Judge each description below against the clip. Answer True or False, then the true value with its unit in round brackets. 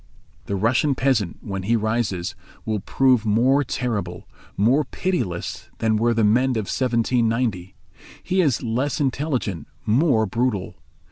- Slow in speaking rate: True (130 wpm)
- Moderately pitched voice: False (115 Hz)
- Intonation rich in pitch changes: False (3.9 semitones)